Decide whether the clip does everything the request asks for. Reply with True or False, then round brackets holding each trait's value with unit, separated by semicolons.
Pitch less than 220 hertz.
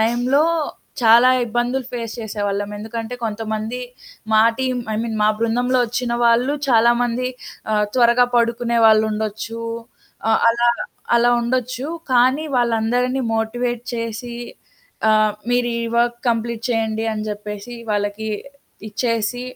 False (235 Hz)